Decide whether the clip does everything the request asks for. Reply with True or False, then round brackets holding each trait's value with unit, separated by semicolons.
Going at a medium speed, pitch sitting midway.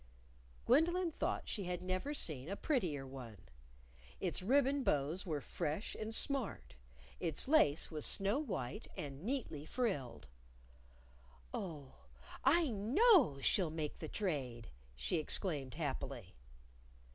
False (120 wpm; 175 Hz)